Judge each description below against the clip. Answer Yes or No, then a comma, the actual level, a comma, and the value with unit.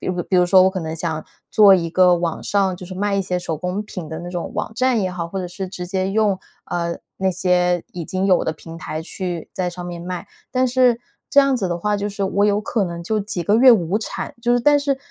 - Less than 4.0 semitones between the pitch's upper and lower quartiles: Yes, average, 2.9 semitones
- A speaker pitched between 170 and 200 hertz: Yes, medium, 185 Hz